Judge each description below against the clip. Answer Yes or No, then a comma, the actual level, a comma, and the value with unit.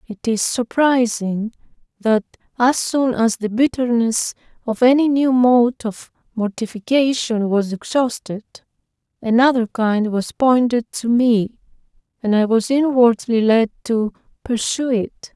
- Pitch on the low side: No, high, 235 Hz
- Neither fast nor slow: No, slow, 120 wpm